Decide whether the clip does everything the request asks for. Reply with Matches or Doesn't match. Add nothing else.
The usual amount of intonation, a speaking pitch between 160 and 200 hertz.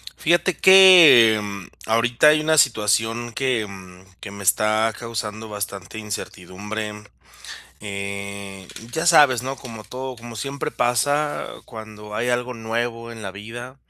Doesn't match